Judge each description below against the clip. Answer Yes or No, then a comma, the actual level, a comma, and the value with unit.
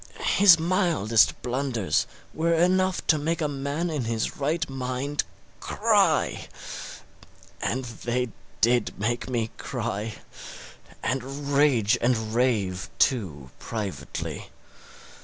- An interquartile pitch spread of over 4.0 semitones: Yes, average, 4.9 semitones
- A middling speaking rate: No, slow, 100 wpm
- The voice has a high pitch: No, low, 130 Hz